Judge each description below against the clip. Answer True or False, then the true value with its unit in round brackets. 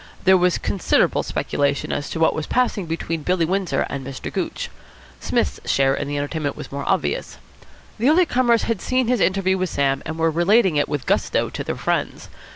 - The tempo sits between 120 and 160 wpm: False (195 wpm)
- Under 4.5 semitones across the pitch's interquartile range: False (5.5 semitones)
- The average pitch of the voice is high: False (170 Hz)